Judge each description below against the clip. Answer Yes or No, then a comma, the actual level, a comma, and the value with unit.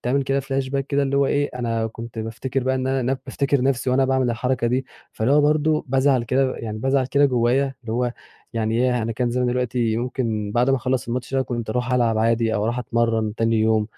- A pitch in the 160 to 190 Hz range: No, low, 125 Hz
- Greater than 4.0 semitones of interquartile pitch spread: No, narrow, 2.5 semitones